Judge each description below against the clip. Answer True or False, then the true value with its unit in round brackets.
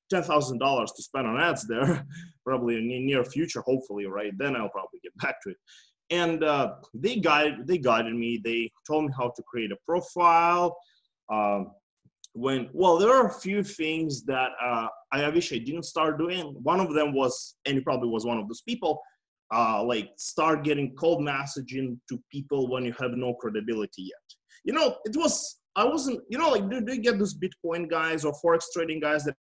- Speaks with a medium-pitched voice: True (150 Hz)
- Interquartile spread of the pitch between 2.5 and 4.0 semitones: False (5.6 semitones)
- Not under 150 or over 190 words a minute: False (200 wpm)